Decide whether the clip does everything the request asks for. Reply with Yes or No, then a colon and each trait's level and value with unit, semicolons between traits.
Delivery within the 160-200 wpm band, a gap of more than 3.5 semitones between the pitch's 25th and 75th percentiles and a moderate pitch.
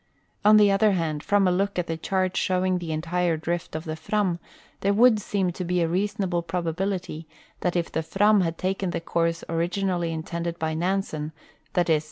No: average, 190 wpm; average, 2.7 semitones; medium, 175 Hz